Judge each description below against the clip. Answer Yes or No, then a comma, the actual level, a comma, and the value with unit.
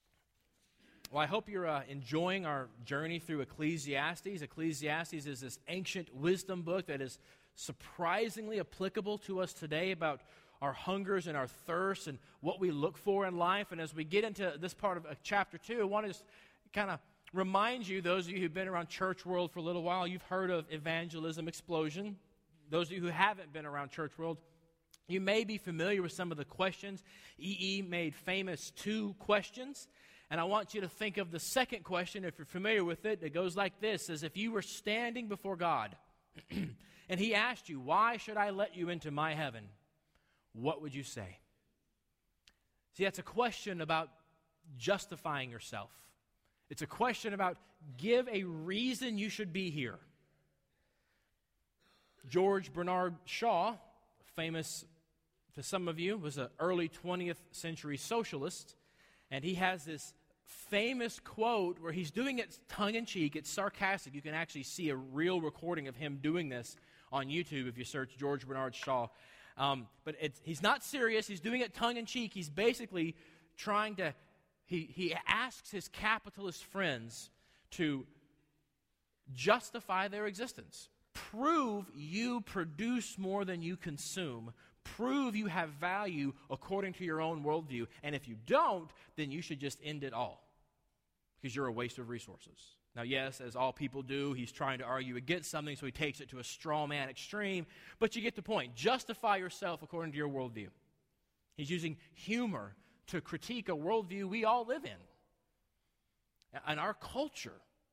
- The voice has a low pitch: No, medium, 175 Hz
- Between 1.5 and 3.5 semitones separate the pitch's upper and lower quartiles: No, average, 5.1 semitones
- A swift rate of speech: No, average, 170 wpm